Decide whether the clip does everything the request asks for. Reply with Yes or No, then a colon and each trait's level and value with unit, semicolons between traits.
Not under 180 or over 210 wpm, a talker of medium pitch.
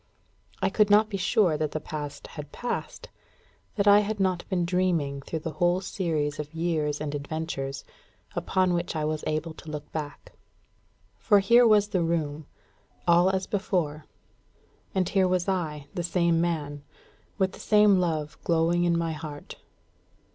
No: average, 160 wpm; medium, 170 Hz